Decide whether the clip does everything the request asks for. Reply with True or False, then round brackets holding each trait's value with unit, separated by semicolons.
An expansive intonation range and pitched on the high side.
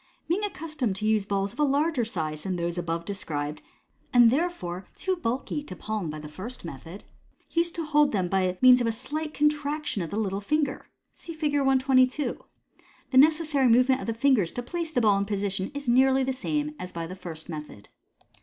True (7.8 semitones; 240 Hz)